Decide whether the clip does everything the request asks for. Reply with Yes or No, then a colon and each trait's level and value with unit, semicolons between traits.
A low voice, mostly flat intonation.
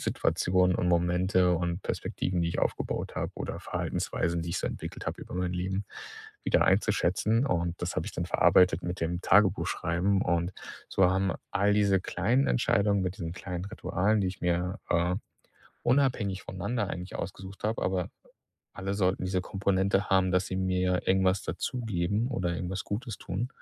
Yes: very low, 95 Hz; narrow, 2.0 semitones